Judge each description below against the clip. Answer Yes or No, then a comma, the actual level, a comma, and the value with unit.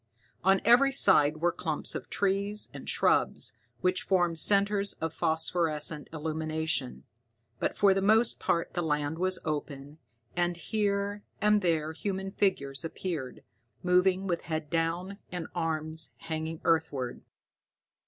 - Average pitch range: Yes, average, 3.5 semitones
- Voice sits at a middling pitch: Yes, medium, 170 Hz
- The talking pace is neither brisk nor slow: No, slow, 130 wpm